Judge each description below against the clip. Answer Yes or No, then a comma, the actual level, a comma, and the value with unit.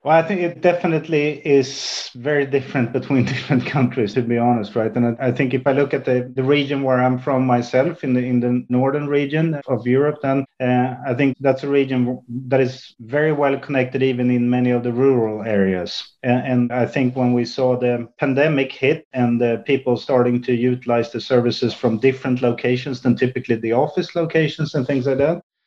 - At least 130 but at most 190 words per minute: No, average, 200 wpm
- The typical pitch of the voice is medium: No, low, 130 Hz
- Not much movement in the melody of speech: Yes, narrow, 2.3 semitones